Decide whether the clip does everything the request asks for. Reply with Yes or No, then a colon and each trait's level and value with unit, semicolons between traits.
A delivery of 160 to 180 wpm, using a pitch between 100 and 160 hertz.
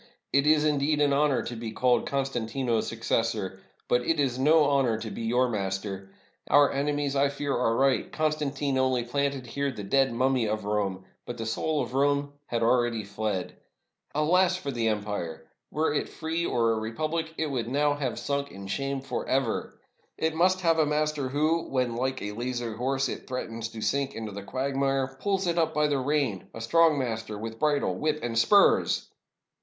No: average, 195 wpm; low, 135 Hz